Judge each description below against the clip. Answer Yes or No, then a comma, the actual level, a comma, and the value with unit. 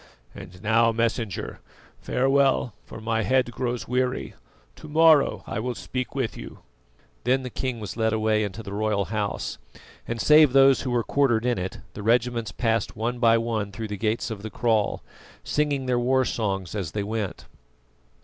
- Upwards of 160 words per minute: Yes, average, 175 wpm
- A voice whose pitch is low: Yes, low, 115 Hz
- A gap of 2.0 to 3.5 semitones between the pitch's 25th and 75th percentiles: Yes, average, 2.9 semitones